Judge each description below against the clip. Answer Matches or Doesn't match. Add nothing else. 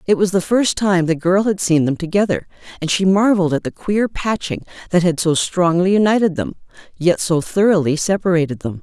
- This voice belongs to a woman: Matches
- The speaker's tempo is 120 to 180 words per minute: Doesn't match